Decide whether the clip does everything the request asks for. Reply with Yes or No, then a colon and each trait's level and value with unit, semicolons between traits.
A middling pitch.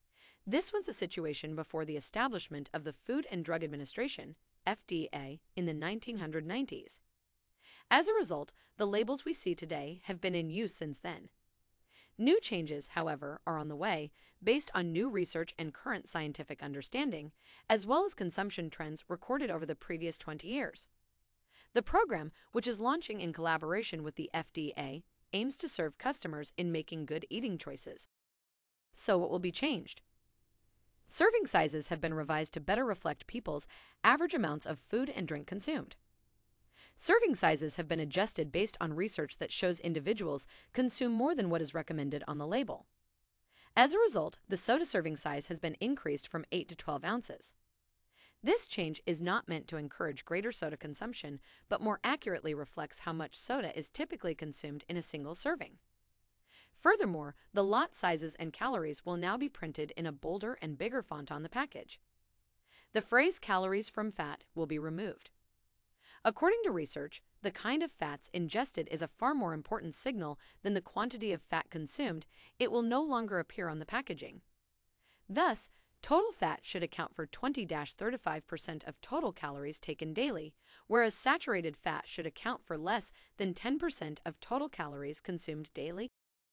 Yes: medium, 175 Hz